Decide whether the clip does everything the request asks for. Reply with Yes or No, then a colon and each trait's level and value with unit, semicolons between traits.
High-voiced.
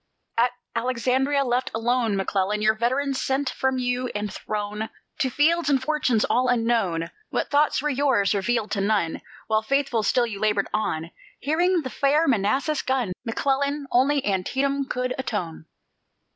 Yes: very high, 250 Hz